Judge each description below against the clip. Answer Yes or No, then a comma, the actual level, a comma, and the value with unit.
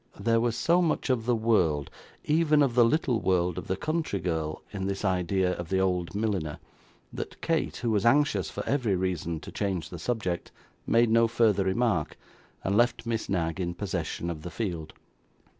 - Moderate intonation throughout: Yes, average, 4.8 semitones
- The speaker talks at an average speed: Yes, average, 185 wpm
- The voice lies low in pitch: Yes, low, 100 Hz